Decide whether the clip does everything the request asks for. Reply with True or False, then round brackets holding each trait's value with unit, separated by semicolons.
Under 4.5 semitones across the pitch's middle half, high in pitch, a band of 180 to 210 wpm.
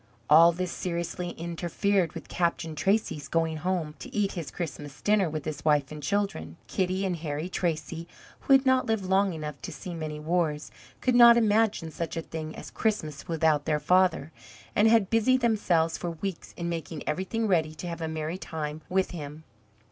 False (3.7 semitones; 170 Hz; 185 wpm)